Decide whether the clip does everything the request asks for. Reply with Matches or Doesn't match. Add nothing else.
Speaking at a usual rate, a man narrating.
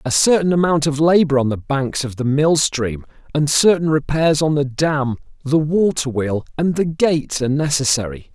Matches